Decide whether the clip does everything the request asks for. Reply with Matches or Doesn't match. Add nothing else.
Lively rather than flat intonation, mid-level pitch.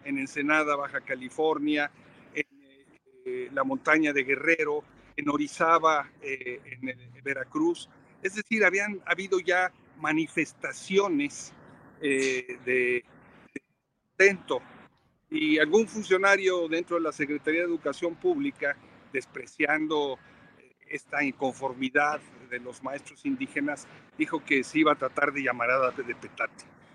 Matches